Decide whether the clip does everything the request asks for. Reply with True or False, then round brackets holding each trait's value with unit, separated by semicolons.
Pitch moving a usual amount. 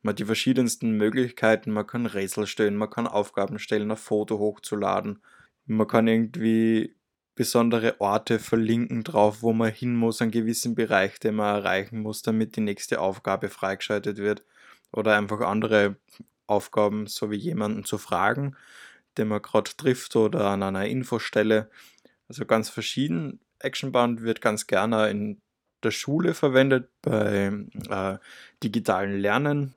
False (2.0 semitones)